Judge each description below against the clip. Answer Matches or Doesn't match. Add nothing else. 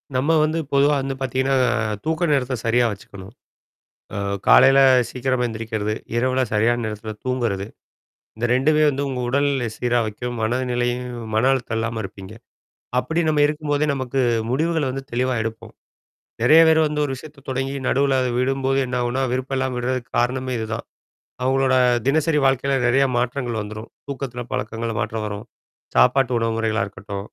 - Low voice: Matches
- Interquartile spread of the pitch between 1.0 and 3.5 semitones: Matches